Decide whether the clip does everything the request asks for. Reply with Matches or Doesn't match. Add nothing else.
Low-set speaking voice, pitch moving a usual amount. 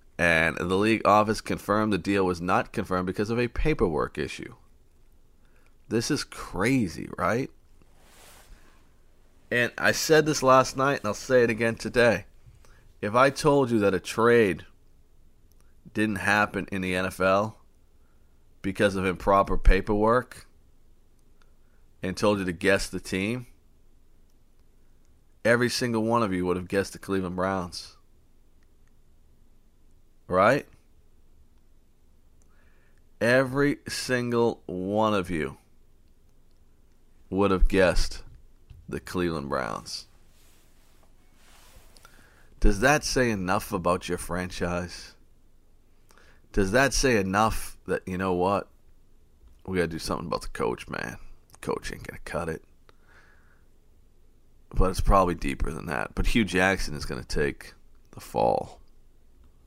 Matches